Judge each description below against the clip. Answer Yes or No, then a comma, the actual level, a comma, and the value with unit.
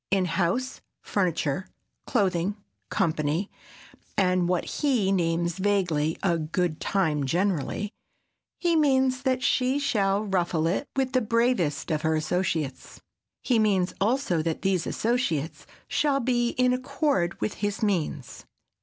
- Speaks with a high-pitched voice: Yes, high, 195 Hz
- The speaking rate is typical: No, slow, 125 wpm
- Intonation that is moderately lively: No, wide, 6.6 semitones